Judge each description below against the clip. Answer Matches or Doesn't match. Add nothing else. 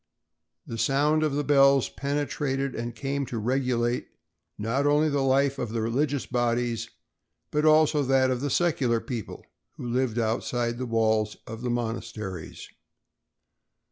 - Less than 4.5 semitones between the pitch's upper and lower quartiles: Matches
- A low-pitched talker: Matches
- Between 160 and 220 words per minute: Doesn't match